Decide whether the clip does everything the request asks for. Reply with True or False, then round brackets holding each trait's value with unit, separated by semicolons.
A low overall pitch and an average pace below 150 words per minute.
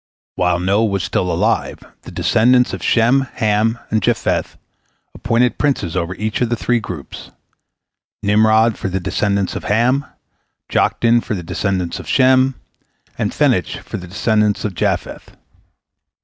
True (110 Hz; 140 wpm)